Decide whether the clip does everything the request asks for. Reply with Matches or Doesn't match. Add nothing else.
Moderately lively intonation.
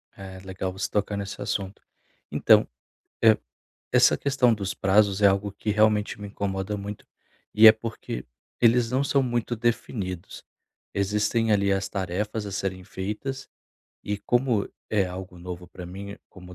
Doesn't match